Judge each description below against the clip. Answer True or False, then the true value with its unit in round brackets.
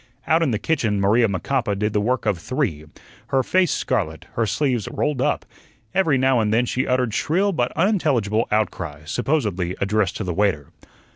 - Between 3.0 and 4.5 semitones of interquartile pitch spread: False (5.0 semitones)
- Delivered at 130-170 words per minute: False (180 wpm)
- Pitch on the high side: False (115 Hz)